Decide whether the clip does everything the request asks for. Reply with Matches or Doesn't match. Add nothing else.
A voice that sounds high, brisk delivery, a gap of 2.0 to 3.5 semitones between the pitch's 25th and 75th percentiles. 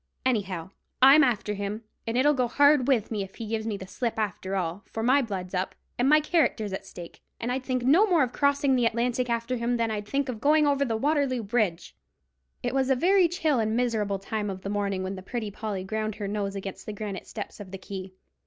Doesn't match